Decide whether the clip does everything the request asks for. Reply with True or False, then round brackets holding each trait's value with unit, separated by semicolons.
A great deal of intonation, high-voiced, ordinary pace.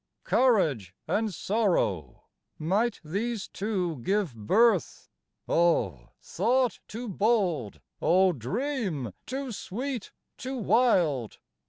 False (7.5 semitones; 195 Hz; 90 wpm)